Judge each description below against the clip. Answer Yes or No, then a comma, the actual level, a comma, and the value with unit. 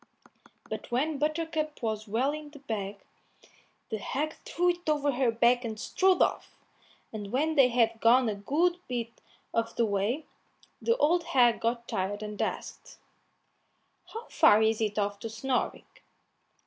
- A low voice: No, high, 245 Hz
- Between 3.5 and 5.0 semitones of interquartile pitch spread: No, wide, 5.6 semitones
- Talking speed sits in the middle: Yes, average, 155 wpm